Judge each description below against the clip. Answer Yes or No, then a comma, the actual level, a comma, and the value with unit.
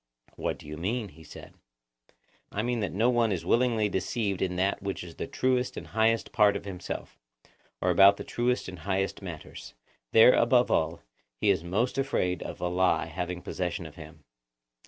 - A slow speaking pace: No, average, 185 wpm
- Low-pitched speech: Yes, very low, 95 Hz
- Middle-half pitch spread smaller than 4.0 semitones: No, average, 4.6 semitones